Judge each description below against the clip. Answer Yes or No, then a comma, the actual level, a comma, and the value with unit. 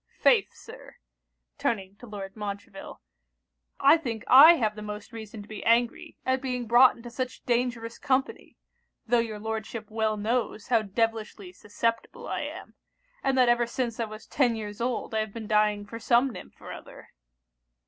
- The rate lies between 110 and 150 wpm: No, average, 170 wpm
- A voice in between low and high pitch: No, high, 225 Hz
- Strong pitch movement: No, narrow, 2.4 semitones